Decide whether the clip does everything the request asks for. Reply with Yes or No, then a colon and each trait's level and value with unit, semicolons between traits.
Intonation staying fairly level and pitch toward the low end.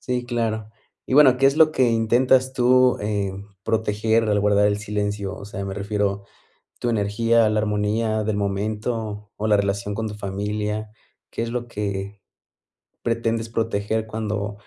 Yes: narrow, 2.0 semitones; low, 110 Hz